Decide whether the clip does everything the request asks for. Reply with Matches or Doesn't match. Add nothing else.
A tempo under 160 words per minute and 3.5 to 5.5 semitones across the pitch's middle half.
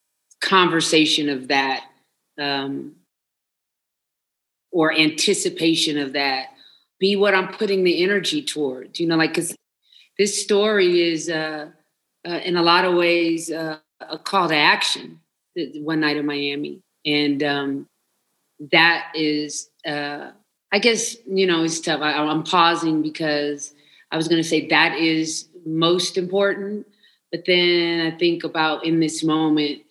Doesn't match